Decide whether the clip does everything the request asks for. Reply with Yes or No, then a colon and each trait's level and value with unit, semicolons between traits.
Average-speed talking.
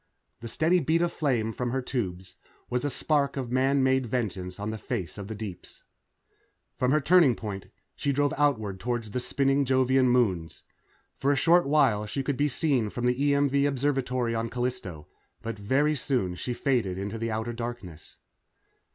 Yes: average, 180 wpm